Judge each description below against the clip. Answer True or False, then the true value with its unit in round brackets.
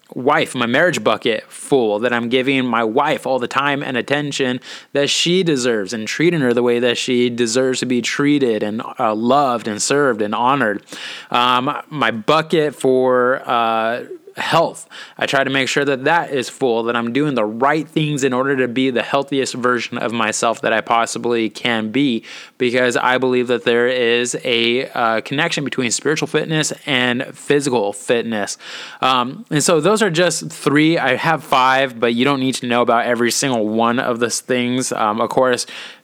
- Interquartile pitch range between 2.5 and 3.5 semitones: True (2.9 semitones)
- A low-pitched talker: True (130 Hz)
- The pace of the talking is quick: False (185 wpm)